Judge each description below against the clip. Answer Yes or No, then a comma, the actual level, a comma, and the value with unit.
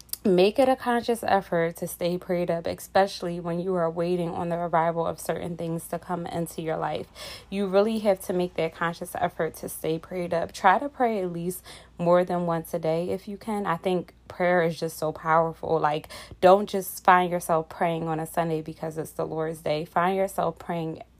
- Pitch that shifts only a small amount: Yes, narrow, 2.0 semitones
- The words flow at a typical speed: No, fast, 210 wpm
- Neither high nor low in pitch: Yes, medium, 175 Hz